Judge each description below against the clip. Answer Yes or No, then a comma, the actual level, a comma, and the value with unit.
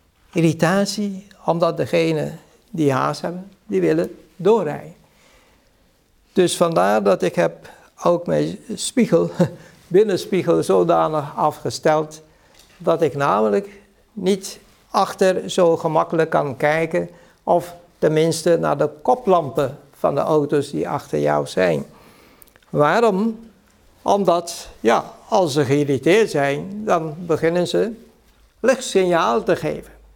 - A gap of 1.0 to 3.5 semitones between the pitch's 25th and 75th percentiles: No, average, 4.0 semitones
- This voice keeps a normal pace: No, slow, 105 wpm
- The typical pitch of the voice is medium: Yes, medium, 170 Hz